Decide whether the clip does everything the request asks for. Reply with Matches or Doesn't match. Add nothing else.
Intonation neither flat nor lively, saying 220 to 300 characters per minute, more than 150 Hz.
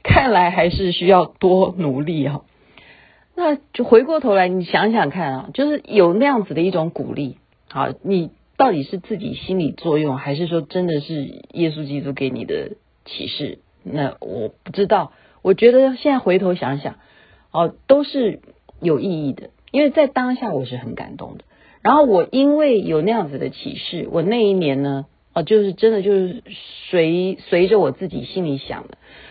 Doesn't match